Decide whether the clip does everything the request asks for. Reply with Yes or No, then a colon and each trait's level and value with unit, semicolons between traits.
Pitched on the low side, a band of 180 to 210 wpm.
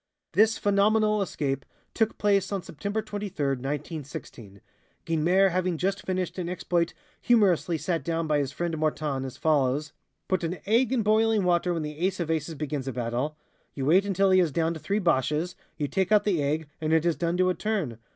No: medium, 170 Hz; average, 190 wpm